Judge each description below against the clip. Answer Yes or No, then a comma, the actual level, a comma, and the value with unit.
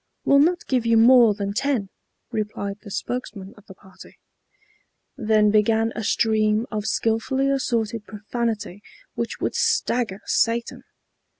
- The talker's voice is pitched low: No, high, 225 Hz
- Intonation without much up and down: Yes, narrow, 2.3 semitones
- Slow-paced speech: Yes, slow, 130 wpm